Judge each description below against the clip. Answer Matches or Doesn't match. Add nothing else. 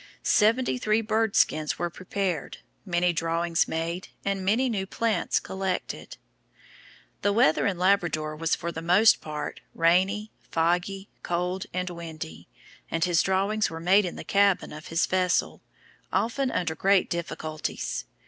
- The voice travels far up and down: Doesn't match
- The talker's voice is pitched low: Doesn't match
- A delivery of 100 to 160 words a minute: Matches